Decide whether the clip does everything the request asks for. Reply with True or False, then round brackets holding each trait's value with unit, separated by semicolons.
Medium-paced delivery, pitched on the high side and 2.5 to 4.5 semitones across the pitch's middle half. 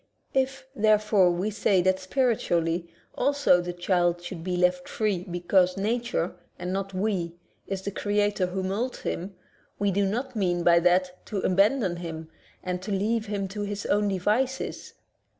True (165 wpm; 195 Hz; 2.9 semitones)